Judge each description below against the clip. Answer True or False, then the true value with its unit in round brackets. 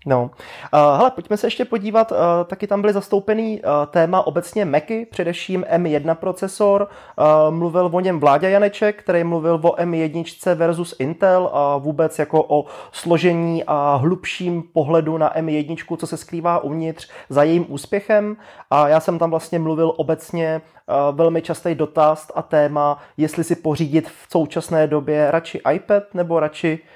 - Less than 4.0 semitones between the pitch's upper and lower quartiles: True (2.6 semitones)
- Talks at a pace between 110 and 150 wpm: True (145 wpm)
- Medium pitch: True (165 Hz)